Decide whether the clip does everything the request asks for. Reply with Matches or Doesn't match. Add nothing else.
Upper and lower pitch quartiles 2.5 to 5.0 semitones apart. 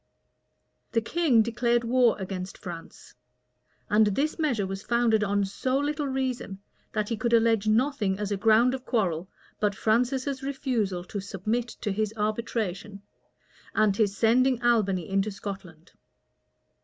Matches